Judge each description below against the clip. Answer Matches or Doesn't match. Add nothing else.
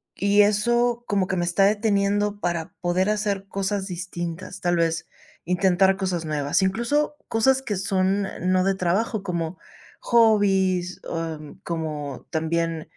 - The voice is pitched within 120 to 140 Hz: Doesn't match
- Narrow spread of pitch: Doesn't match